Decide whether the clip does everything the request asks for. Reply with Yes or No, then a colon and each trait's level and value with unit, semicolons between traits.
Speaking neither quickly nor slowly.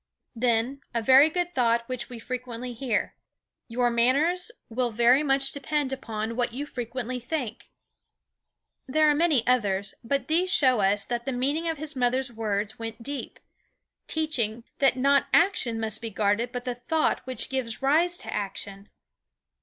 Yes: average, 160 wpm